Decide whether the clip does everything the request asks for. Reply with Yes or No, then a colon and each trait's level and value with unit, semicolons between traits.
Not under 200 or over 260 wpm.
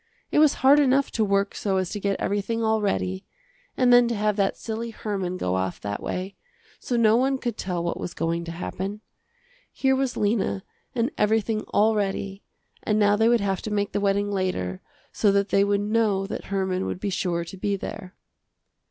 Yes: fast, 205 wpm